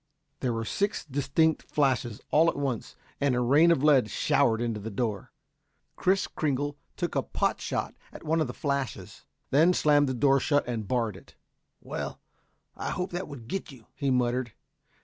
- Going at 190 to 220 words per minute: No, average, 180 wpm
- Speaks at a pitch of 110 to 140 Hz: Yes, low, 135 Hz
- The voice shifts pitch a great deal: No, average, 4.0 semitones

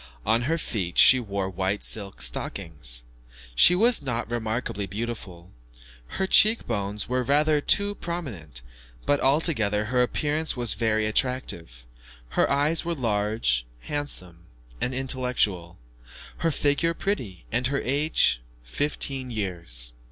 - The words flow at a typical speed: No, slow, 125 wpm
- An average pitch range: No, wide, 7.2 semitones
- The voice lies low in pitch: Yes, low, 115 Hz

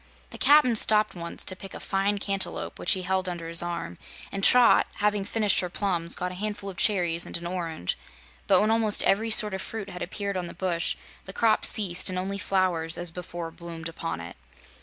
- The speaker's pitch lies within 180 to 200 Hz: Yes, medium, 185 Hz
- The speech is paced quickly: Yes, fast, 210 wpm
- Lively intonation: No, average, 3.0 semitones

